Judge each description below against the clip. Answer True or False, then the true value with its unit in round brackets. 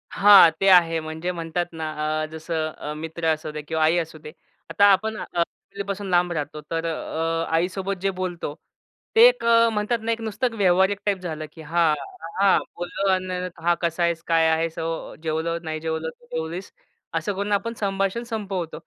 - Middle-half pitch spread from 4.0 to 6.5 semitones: False (3.5 semitones)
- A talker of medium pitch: True (170 Hz)